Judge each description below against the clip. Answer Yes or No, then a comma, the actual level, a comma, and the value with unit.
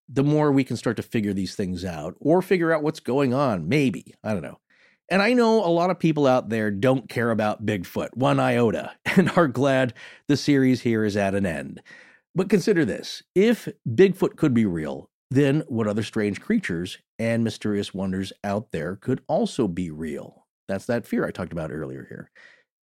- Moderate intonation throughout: No, wide, 7.4 semitones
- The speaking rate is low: No, average, 195 wpm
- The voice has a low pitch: Yes, low, 120 Hz